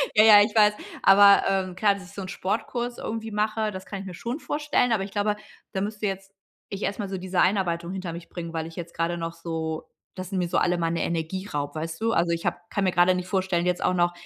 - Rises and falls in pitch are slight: No, average, 3.2 semitones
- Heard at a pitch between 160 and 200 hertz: Yes, high, 190 Hz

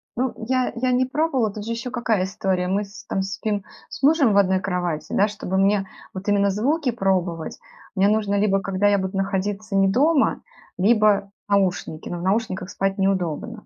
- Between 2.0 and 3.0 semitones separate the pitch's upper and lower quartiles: Yes, average, 2.7 semitones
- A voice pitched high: Yes, high, 200 Hz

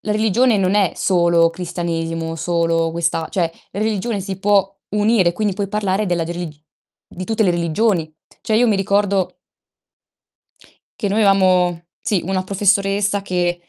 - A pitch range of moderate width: Yes, average, 3.1 semitones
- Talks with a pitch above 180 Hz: Yes, high, 190 Hz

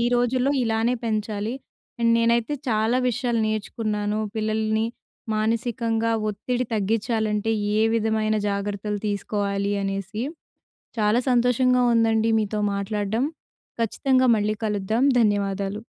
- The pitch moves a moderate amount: No, narrow, 1.9 semitones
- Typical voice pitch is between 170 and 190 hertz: No, high, 220 Hz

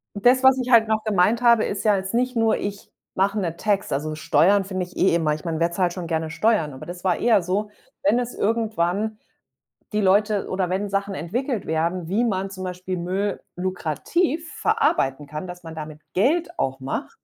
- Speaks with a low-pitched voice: No, high, 195 Hz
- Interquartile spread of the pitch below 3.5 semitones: No, average, 4.2 semitones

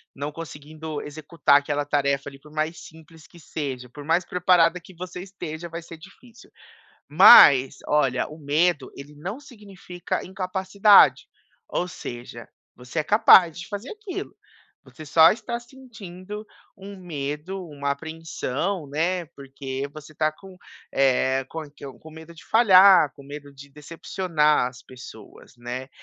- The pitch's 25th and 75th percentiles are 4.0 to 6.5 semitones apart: Yes, average, 4.4 semitones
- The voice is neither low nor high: Yes, medium, 160 Hz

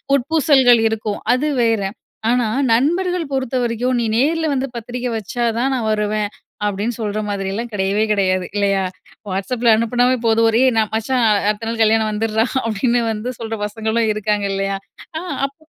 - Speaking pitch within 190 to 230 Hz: Yes, high, 225 Hz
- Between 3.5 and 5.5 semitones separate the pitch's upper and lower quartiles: No, average, 2.9 semitones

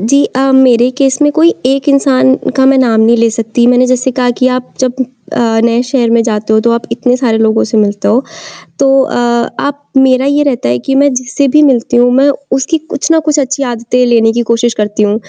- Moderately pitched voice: No, very high, 250 Hz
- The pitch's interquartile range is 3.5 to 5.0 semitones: No, average, 2.7 semitones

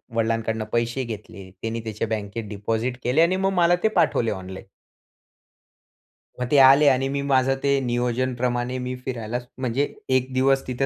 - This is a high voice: No, low, 125 Hz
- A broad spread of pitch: No, average, 2.9 semitones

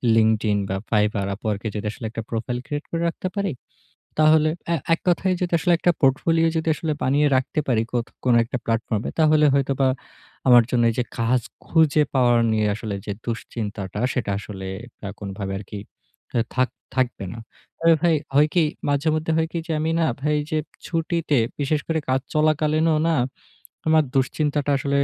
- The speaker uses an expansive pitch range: Yes, wide, 5.7 semitones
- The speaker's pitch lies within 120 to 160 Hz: Yes, low, 135 Hz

